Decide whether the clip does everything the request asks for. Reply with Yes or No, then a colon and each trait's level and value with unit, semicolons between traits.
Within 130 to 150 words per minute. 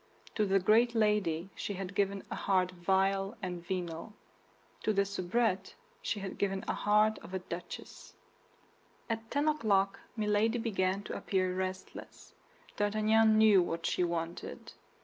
Yes: average, 145 wpm